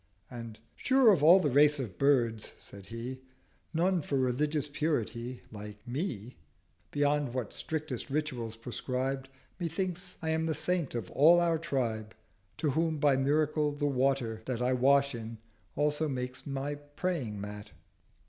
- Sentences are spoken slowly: No, average, 150 wpm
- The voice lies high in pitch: No, medium, 140 Hz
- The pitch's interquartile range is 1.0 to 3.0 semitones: No, average, 4.2 semitones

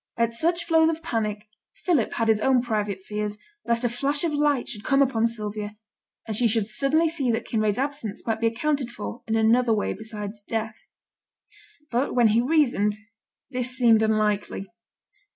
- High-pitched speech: Yes, high, 230 Hz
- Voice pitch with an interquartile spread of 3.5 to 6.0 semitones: Yes, average, 4.1 semitones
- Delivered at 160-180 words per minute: Yes, average, 170 wpm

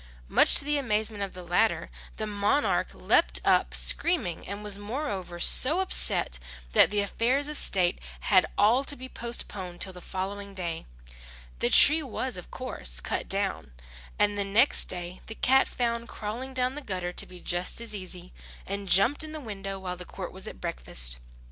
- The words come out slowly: No, average, 180 wpm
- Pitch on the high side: Yes, high, 205 Hz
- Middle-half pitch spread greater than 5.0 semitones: Yes, wide, 5.6 semitones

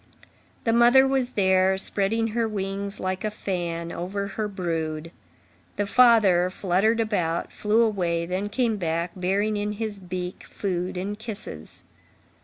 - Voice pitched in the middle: No, high, 195 Hz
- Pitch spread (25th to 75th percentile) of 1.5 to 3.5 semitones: Yes, average, 3.2 semitones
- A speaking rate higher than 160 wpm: No, average, 140 wpm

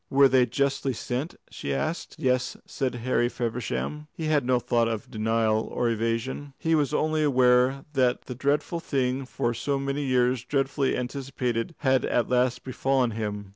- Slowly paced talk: No, average, 165 wpm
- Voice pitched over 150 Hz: No, low, 130 Hz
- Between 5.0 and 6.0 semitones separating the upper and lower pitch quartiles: No, narrow, 2.4 semitones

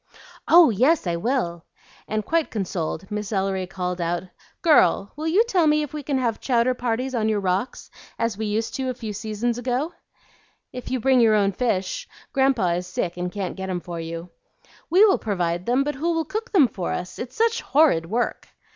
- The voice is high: Yes, high, 225 Hz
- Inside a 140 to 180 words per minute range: No, average, 200 wpm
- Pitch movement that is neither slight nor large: No, wide, 6.5 semitones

